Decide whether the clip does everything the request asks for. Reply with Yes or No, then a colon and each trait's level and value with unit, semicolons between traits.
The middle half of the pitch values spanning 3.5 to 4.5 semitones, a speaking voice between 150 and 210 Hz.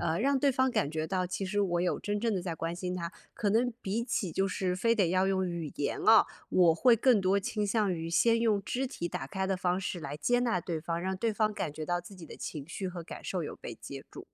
Yes: average, 3.9 semitones; medium, 185 Hz